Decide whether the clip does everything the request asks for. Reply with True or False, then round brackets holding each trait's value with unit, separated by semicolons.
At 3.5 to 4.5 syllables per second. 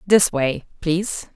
True (3.7 syllables/s)